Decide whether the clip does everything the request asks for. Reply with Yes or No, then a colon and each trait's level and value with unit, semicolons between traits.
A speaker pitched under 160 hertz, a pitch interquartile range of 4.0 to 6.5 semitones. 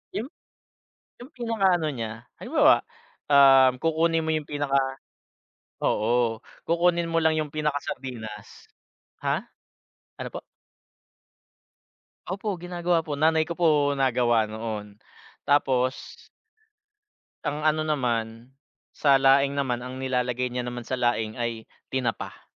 Yes: low, 135 Hz; average, 4.8 semitones